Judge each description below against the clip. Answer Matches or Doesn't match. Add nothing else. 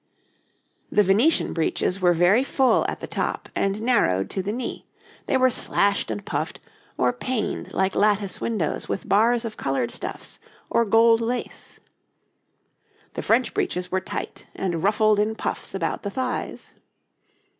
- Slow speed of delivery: Doesn't match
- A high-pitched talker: Matches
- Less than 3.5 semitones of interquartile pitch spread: Doesn't match